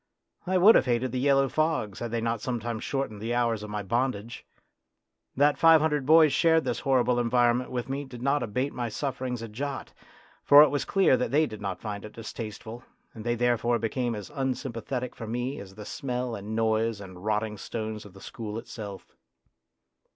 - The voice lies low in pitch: Yes, low, 120 Hz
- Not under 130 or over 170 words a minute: No, average, 195 wpm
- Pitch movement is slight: No, average, 3.6 semitones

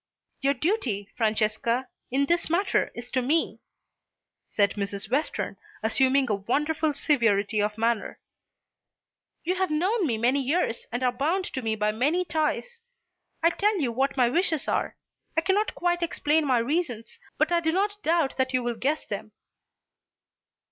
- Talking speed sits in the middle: Yes, average, 160 wpm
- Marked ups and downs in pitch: Yes, wide, 6.2 semitones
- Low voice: No, very high, 275 Hz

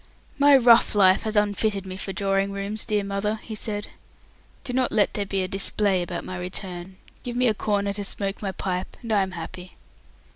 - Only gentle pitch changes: Yes, narrow, 2.0 semitones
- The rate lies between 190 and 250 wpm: Yes, fast, 205 wpm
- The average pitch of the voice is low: No, high, 200 Hz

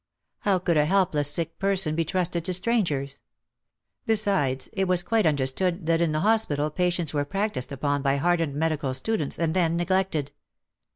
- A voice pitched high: No, medium, 165 Hz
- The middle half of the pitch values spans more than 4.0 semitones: Yes, average, 4.4 semitones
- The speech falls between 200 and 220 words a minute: No, average, 170 wpm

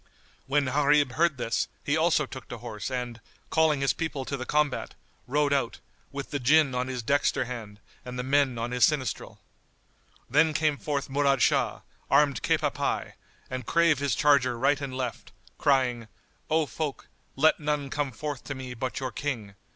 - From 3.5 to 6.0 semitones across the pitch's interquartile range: No, average, 2.9 semitones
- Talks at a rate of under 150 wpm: No, average, 180 wpm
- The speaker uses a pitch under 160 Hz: Yes, low, 135 Hz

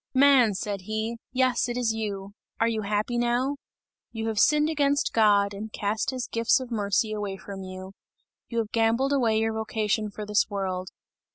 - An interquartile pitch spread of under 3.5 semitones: Yes, average, 2.8 semitones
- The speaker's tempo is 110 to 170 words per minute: No, average, 180 wpm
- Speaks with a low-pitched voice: No, high, 220 Hz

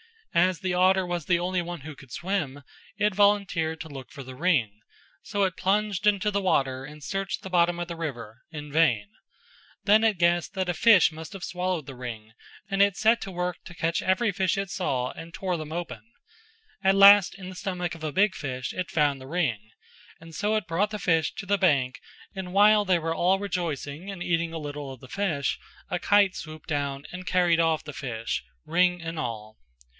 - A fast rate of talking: Yes, fast, 210 wpm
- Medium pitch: Yes, medium, 175 Hz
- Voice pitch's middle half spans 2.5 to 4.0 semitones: No, average, 4.5 semitones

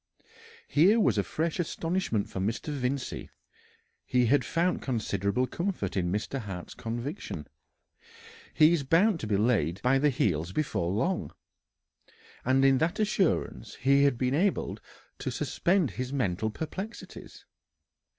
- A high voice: No, low, 135 Hz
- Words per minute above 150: No, slow, 135 wpm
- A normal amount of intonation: No, wide, 7.0 semitones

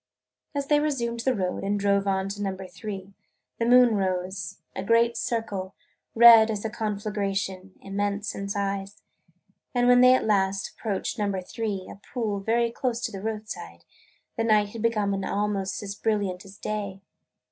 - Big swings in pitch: No, average, 2.7 semitones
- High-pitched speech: Yes, high, 205 Hz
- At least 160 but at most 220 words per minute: Yes, average, 170 wpm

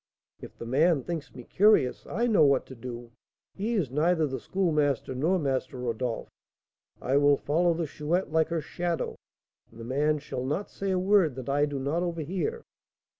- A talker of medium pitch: Yes, medium, 150 Hz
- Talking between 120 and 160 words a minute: No, average, 180 wpm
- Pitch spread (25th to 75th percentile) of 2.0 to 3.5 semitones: No, average, 4.9 semitones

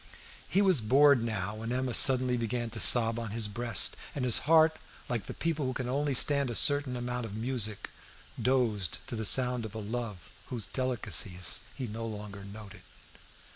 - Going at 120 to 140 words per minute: No, average, 180 wpm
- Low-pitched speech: Yes, low, 120 Hz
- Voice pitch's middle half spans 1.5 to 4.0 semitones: Yes, average, 3.2 semitones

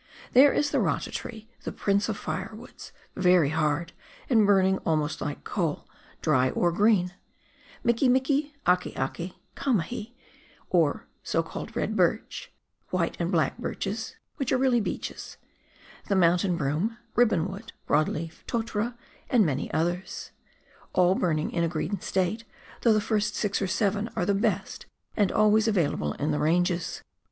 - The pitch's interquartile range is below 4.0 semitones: No, average, 4.7 semitones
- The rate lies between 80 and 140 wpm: No, average, 150 wpm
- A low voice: No, high, 190 Hz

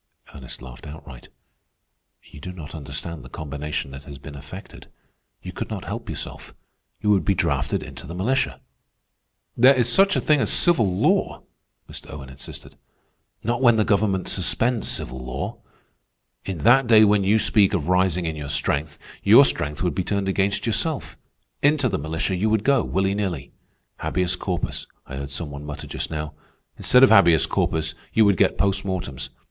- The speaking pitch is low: Yes, very low, 90 Hz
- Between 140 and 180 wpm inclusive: Yes, average, 175 wpm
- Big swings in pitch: Yes, wide, 6.5 semitones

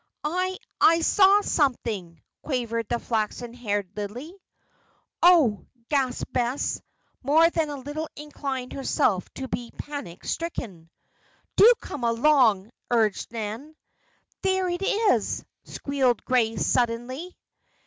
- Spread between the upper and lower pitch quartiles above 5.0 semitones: Yes, wide, 5.4 semitones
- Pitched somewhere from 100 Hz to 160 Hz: No, very high, 255 Hz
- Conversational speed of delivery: No, slow, 110 wpm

